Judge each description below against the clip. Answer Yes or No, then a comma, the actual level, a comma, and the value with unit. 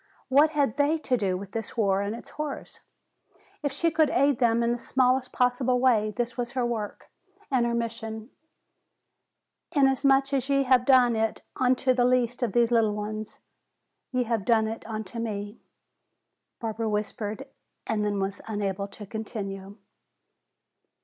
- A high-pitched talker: Yes, high, 235 Hz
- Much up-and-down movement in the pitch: No, average, 3.2 semitones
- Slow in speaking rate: No, average, 155 wpm